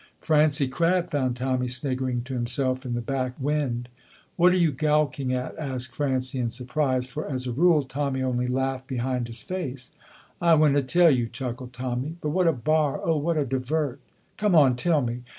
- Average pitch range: Yes, average, 3.1 semitones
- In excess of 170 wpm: Yes, average, 185 wpm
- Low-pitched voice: Yes, low, 130 Hz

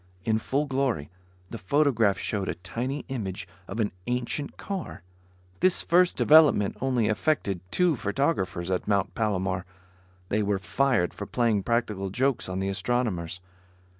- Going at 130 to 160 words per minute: Yes, average, 140 wpm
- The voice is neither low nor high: No, low, 110 Hz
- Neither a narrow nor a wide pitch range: No, wide, 5.8 semitones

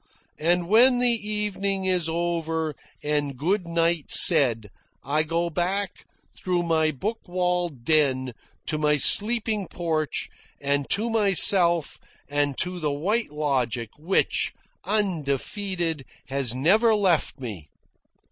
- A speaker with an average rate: No, slow, 120 wpm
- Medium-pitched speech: Yes, medium, 170 Hz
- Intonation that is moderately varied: Yes, average, 4.9 semitones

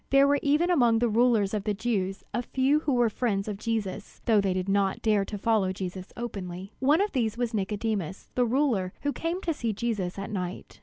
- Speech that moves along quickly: Yes, fast, 215 wpm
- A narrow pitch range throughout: No, average, 4.1 semitones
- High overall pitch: Yes, high, 220 Hz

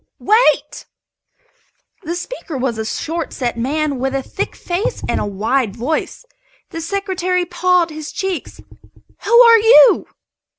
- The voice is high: Yes, very high, 335 Hz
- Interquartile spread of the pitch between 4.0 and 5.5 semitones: No, wide, 6.3 semitones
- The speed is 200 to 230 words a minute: No, slow, 135 wpm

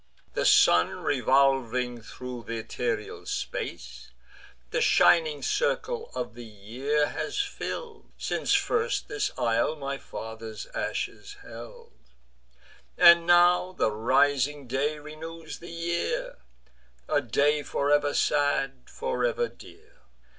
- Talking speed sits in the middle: No, slow, 115 wpm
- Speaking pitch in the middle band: Yes, medium, 150 Hz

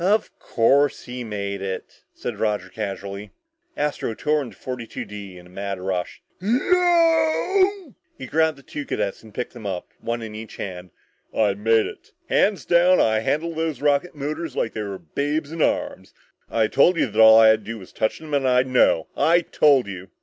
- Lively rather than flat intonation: Yes, wide, 7.3 semitones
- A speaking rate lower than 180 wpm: No, average, 195 wpm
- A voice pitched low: Yes, low, 125 Hz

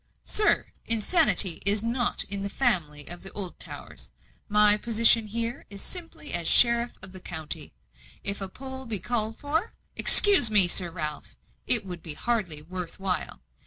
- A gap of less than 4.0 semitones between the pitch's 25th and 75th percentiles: No, average, 4.8 semitones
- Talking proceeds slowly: No, average, 160 wpm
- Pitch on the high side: Yes, high, 205 Hz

